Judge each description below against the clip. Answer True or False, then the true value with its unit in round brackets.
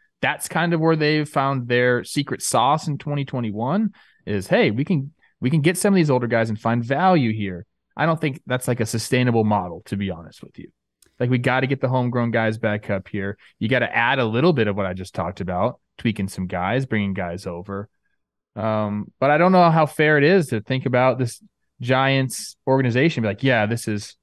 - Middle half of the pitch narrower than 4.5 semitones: False (5.0 semitones)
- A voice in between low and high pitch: False (125 Hz)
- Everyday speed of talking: False (225 wpm)